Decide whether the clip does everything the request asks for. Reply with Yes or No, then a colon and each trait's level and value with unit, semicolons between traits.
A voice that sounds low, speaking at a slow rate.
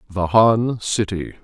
Yes: low, 105 Hz; slow, 125 wpm